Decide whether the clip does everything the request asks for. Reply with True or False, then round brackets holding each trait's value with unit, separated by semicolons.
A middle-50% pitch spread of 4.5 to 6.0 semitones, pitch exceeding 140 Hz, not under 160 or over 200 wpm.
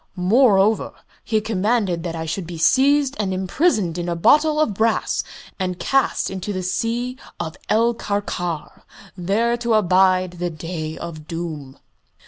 False (4.9 semitones; 190 Hz; 145 wpm)